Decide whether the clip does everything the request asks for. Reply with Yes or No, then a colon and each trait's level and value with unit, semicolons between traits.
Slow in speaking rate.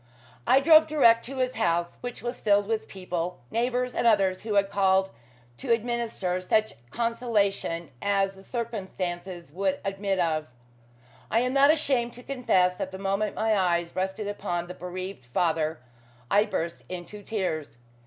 No: average, 155 wpm